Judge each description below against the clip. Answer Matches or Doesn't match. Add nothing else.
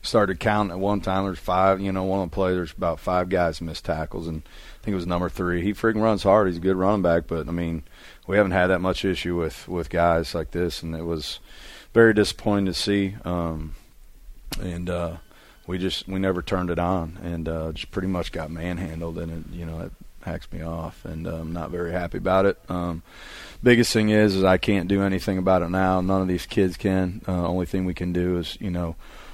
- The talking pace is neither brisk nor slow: Doesn't match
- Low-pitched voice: Matches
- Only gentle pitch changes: Matches